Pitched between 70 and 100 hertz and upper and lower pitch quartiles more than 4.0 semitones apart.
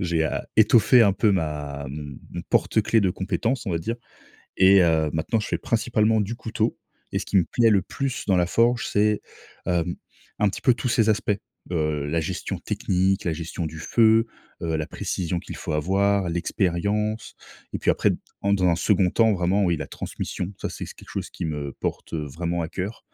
Yes: very low, 95 Hz; average, 4.5 semitones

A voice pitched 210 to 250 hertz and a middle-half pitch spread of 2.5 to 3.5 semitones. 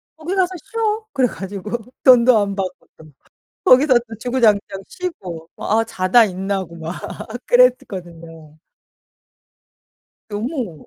No: high, 215 Hz; wide, 5.5 semitones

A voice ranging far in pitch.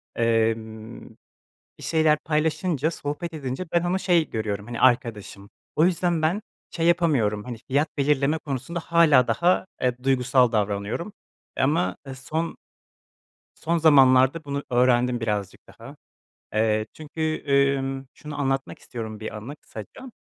Yes: wide, 5.8 semitones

